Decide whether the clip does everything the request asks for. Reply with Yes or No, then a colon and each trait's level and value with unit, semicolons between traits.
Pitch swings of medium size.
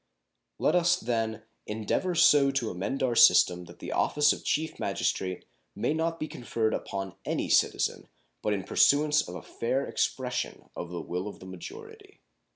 No: wide, 7.9 semitones